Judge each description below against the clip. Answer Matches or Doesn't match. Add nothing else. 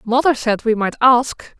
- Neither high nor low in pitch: Doesn't match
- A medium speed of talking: Matches